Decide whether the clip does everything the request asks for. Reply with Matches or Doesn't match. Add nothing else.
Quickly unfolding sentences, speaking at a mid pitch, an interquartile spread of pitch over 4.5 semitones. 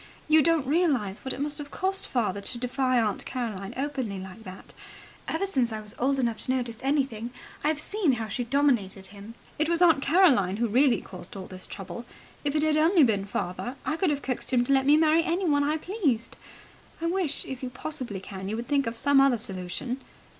Doesn't match